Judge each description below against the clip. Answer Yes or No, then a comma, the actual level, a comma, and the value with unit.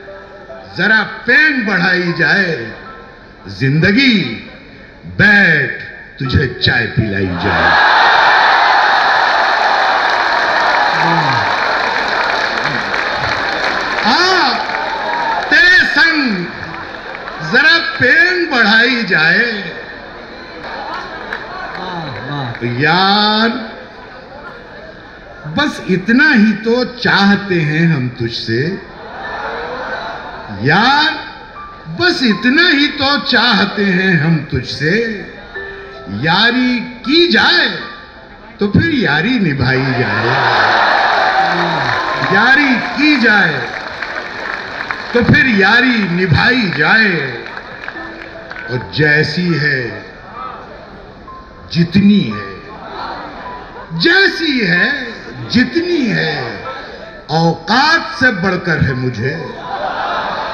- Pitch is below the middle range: No, high, 200 Hz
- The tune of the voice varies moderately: No, wide, 7.8 semitones